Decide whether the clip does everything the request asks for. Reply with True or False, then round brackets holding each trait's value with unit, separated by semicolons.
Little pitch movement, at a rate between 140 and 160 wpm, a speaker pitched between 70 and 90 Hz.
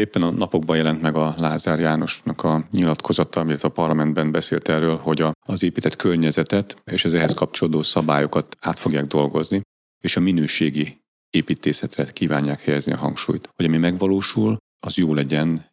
True (1.7 semitones; 155 wpm; 80 Hz)